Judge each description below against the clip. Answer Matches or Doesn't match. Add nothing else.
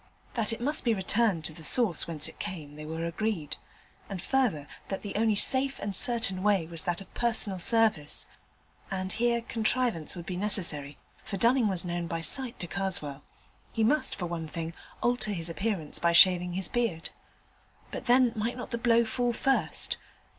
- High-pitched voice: Matches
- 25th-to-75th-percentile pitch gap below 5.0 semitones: Doesn't match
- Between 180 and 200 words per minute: Matches